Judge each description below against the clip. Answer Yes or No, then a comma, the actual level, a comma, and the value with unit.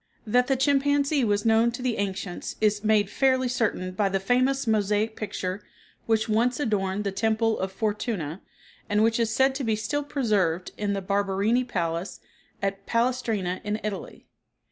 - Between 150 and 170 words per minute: Yes, average, 165 wpm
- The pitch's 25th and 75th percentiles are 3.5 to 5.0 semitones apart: Yes, average, 3.8 semitones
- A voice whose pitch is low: No, high, 215 Hz